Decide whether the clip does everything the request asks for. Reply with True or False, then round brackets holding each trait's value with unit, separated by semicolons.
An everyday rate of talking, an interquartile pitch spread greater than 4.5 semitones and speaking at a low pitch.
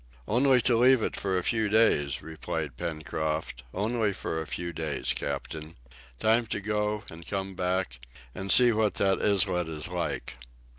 True (160 wpm; 5.3 semitones; 95 Hz)